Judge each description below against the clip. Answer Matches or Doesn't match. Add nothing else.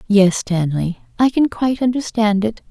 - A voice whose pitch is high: Matches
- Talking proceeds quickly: Doesn't match